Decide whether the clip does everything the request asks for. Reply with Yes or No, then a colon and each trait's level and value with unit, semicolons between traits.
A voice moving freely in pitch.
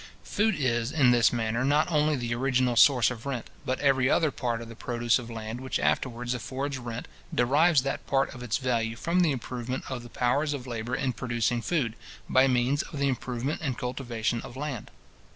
No: narrow, 2.6 semitones